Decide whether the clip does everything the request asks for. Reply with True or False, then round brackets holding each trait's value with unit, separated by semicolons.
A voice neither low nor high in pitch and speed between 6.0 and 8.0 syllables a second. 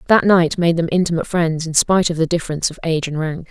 True (165 Hz; 7.0 syllables/s)